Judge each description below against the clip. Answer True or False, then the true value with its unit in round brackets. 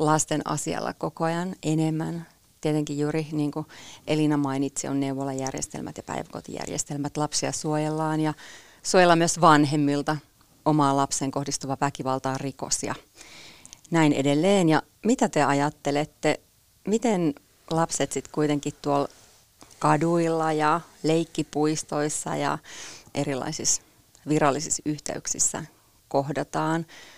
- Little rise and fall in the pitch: True (1.9 semitones)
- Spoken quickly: False (100 wpm)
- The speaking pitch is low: False (150 Hz)